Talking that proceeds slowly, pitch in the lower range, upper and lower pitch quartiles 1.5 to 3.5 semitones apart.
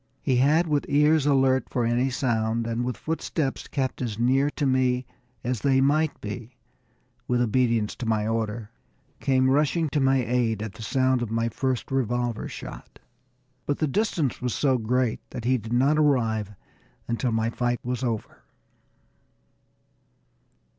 No: average, 155 wpm; low, 125 Hz; average, 2.7 semitones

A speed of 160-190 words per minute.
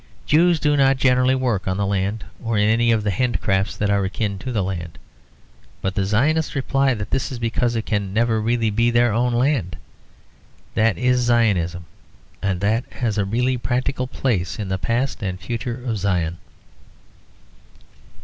Yes: average, 175 wpm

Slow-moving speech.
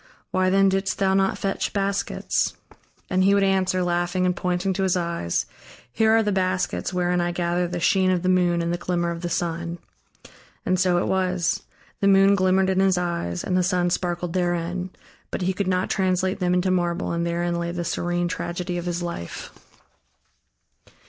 No: average, 190 wpm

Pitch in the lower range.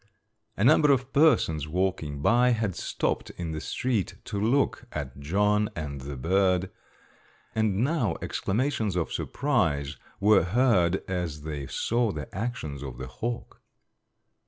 Yes: very low, 95 Hz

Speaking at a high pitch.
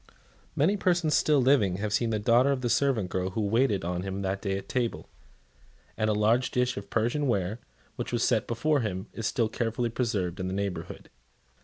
No: low, 115 Hz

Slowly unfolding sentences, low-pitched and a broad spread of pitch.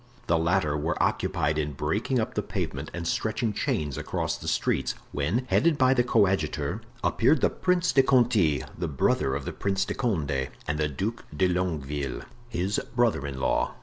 No: average, 180 wpm; very low, 90 Hz; wide, 7.7 semitones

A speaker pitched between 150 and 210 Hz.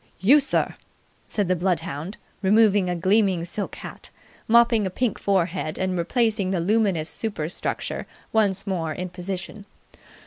Yes: high, 190 Hz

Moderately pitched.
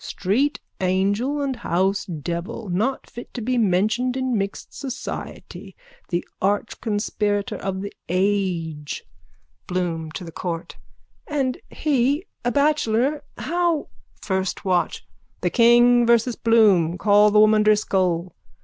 No: high, 210 Hz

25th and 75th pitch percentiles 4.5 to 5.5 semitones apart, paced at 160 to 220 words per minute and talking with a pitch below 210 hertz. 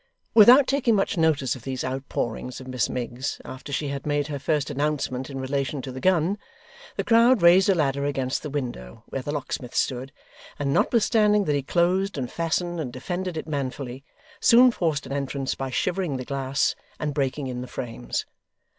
Yes: average, 4.8 semitones; average, 185 wpm; medium, 140 Hz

